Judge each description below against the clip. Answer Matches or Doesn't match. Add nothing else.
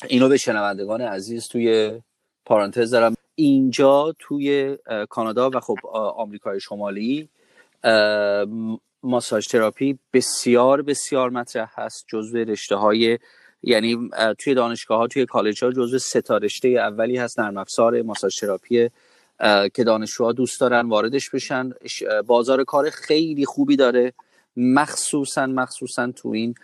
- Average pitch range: Matches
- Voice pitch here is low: Matches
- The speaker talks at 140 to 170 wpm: Doesn't match